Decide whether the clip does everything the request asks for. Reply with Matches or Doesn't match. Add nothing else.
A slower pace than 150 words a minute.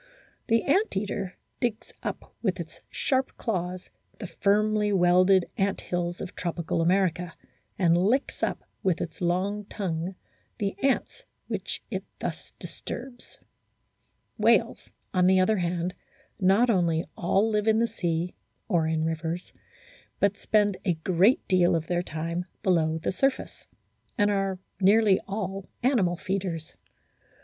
Matches